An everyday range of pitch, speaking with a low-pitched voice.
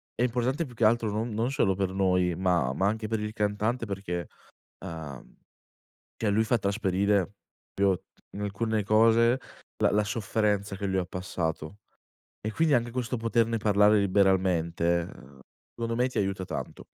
Yes: average, 3.3 semitones; low, 105 Hz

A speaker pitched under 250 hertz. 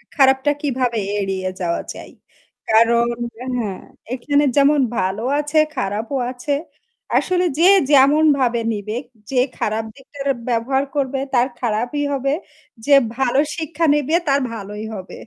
No: very high, 260 Hz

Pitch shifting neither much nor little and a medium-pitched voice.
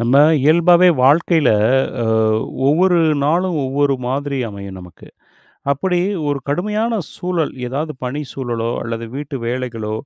No: wide, 5.8 semitones; medium, 145 Hz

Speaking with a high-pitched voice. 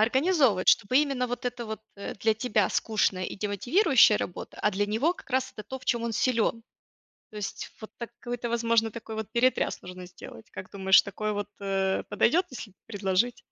Yes: high, 225 Hz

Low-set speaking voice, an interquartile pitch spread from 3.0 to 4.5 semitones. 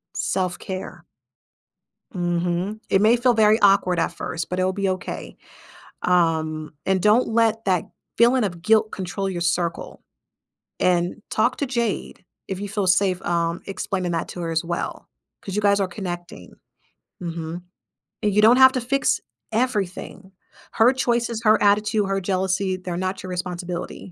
No: high, 190 Hz; average, 3.5 semitones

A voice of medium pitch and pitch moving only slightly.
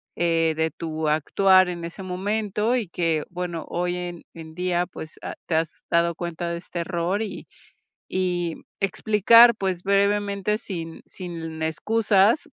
No: medium, 180 Hz; average, 3.0 semitones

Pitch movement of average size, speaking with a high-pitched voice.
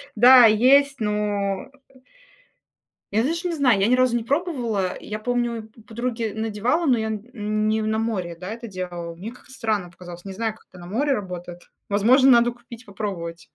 Yes: average, 3.7 semitones; high, 220 Hz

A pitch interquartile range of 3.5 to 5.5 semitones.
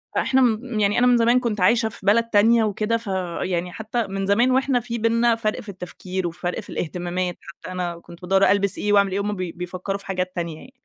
Yes: average, 4.0 semitones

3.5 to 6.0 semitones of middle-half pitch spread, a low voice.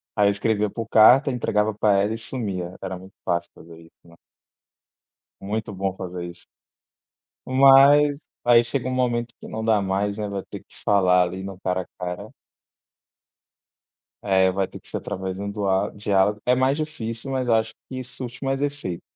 Yes: average, 4.5 semitones; low, 105 Hz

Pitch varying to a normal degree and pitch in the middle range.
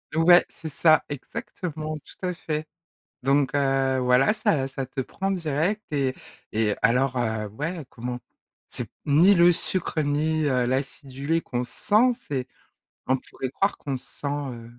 Yes: average, 3.9 semitones; medium, 145 Hz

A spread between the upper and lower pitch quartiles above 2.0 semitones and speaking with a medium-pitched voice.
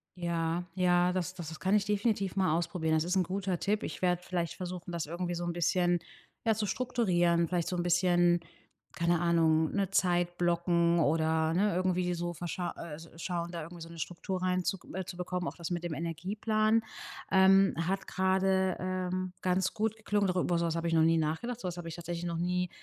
No: narrow, 1.7 semitones; medium, 175 Hz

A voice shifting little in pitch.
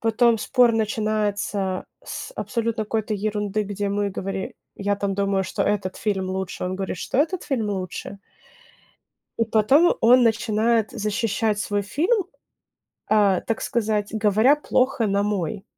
Yes: narrow, 2.3 semitones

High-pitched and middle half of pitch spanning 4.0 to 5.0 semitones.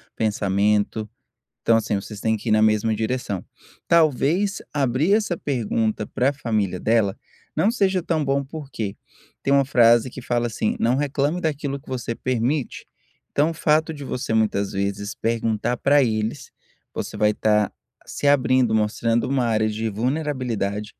No: low, 120 Hz; average, 4.6 semitones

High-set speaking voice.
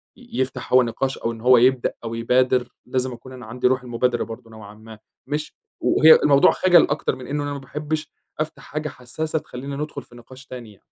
No: low, 130 Hz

